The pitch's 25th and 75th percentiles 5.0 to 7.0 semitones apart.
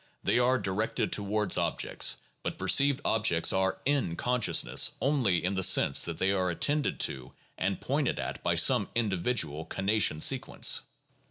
Yes: wide, 5.4 semitones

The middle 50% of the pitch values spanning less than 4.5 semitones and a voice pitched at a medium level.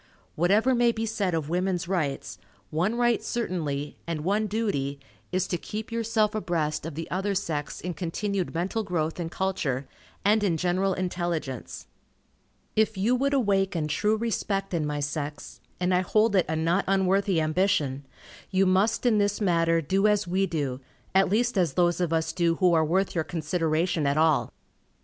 Yes: average, 4.1 semitones; medium, 180 Hz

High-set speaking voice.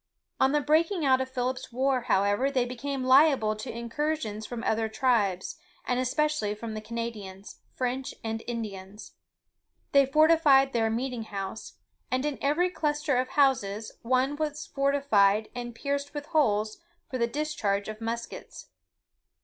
Yes: very high, 255 Hz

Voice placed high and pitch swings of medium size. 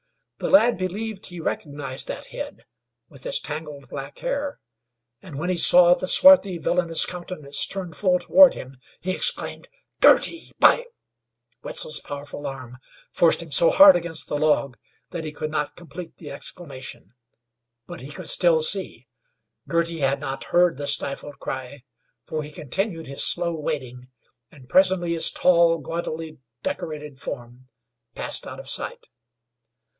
No: medium, 165 Hz; average, 4.5 semitones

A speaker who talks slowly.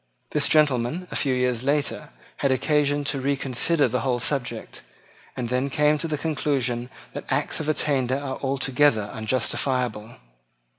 No: average, 145 wpm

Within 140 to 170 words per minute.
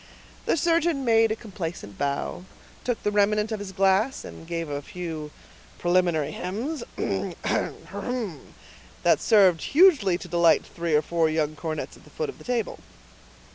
Yes: average, 150 wpm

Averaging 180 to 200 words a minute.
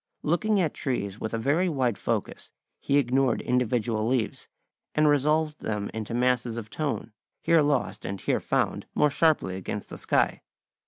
No: average, 160 wpm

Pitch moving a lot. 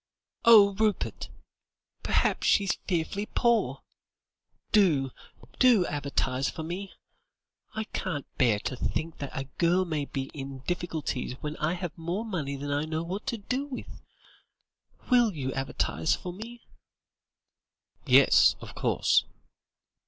Yes: wide, 6.2 semitones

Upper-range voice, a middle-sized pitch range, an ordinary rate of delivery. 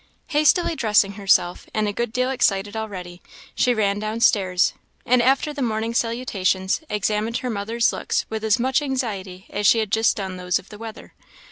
Yes: high, 220 Hz; average, 3.2 semitones; average, 180 wpm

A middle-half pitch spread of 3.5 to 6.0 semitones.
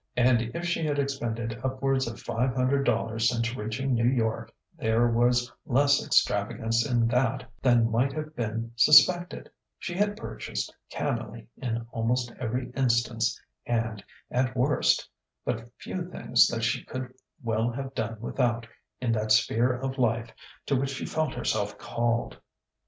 No: narrow, 2.5 semitones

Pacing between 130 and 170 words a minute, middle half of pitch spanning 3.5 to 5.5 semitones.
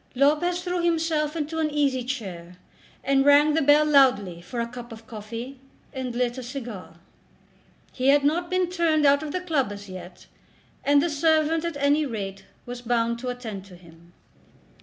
No: average, 180 wpm; average, 4.9 semitones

